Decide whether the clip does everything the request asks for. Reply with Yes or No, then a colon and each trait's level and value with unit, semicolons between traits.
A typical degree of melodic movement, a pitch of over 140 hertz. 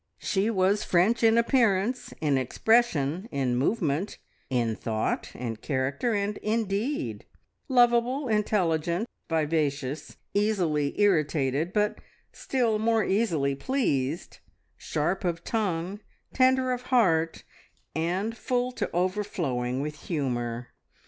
No: wide, 7.7 semitones; medium, 185 Hz